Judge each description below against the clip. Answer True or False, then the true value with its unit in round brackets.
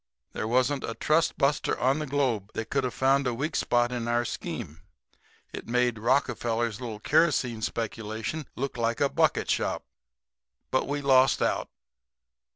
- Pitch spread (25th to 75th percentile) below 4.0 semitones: True (3.1 semitones)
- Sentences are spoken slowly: False (160 wpm)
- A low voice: True (125 Hz)